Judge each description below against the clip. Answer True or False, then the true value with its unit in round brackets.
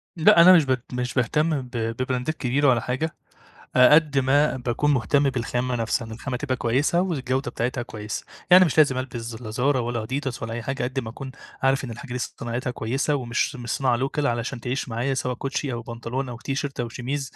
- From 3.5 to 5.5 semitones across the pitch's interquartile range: False (2.8 semitones)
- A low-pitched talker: True (130 Hz)